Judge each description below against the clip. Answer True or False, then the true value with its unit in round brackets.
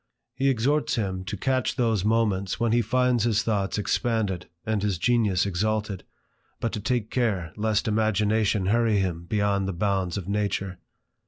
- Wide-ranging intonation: False (2.8 semitones)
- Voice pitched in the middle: False (105 Hz)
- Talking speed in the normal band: True (160 wpm)